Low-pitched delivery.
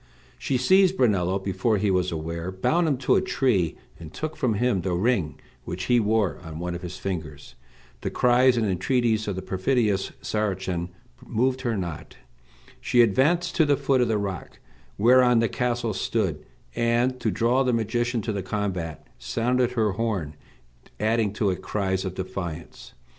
Yes: low, 105 Hz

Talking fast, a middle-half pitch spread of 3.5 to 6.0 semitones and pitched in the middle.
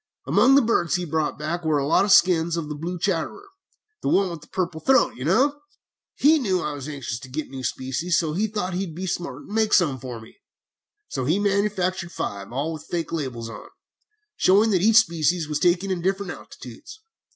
Yes: fast, 215 wpm; average, 4.5 semitones; medium, 170 Hz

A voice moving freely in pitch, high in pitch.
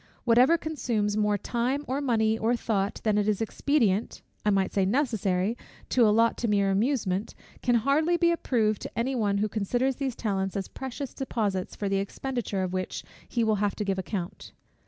No: average, 4.0 semitones; high, 220 Hz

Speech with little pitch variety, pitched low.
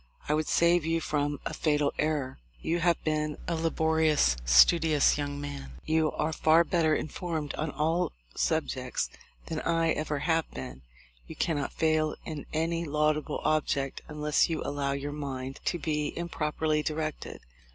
No: narrow, 1.8 semitones; medium, 155 Hz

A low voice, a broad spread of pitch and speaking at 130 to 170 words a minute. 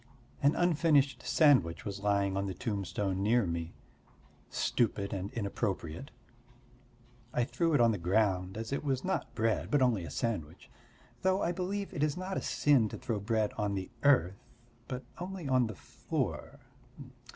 Yes: low, 115 Hz; wide, 6.5 semitones; average, 160 wpm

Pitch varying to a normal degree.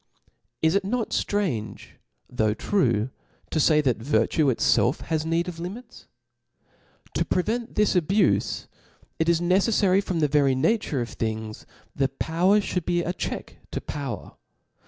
No: wide, 6.3 semitones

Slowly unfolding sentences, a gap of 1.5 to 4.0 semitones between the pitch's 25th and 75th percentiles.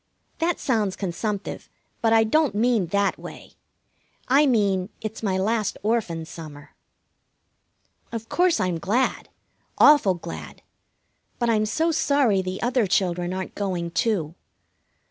No: slow, 125 wpm; average, 4.4 semitones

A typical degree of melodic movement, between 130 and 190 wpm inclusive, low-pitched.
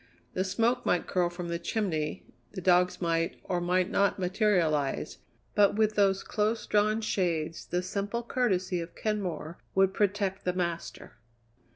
No: average, 3.0 semitones; average, 150 wpm; medium, 185 Hz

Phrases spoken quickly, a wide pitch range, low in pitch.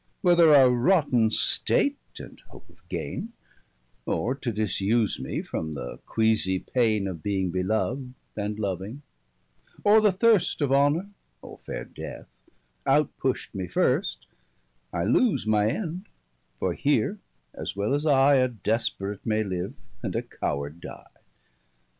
No: average, 140 wpm; wide, 6.5 semitones; low, 115 Hz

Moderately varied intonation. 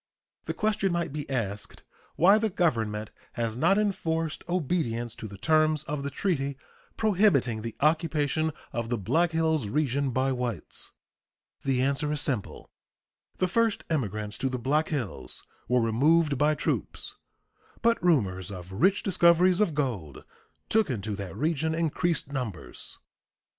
No: wide, 6.2 semitones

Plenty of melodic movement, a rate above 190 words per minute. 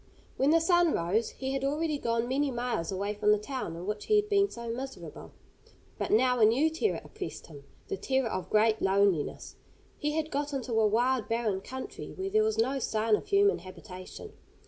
Yes: wide, 6.2 semitones; average, 200 wpm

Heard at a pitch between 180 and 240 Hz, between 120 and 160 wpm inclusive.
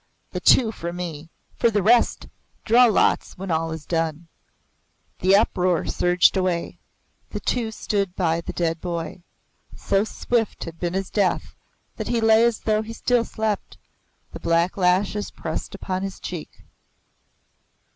Yes: medium, 185 Hz; average, 150 wpm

